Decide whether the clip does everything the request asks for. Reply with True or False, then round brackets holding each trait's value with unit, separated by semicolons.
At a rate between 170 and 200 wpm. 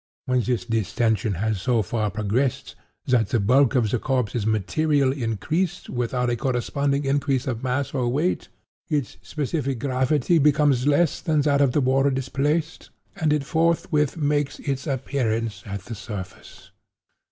False (150 wpm)